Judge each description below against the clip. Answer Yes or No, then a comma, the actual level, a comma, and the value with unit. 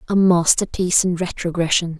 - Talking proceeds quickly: No, slow, 120 wpm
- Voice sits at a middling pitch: Yes, medium, 175 Hz